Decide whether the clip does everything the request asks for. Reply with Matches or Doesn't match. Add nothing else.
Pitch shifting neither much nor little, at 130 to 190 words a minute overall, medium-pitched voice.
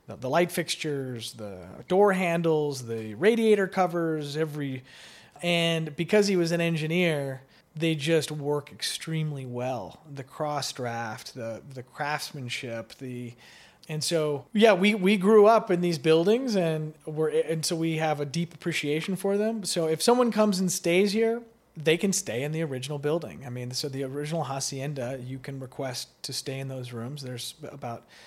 Matches